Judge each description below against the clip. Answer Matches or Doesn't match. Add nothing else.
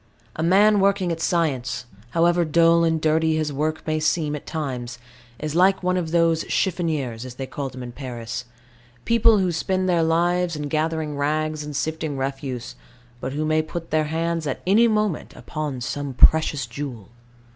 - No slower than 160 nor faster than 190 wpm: Matches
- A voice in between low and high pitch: Matches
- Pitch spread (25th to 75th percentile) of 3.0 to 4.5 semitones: Matches